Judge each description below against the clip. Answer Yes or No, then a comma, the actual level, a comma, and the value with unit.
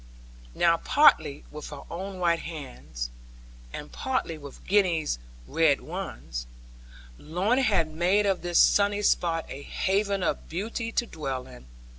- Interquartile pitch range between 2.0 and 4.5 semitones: No, average, 5.0 semitones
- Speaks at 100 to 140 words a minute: Yes, slow, 135 wpm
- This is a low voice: No, medium, 170 Hz